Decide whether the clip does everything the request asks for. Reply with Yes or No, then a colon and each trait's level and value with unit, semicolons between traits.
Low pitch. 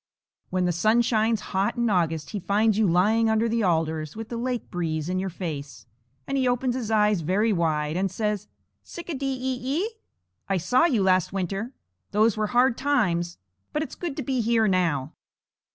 No: high, 210 Hz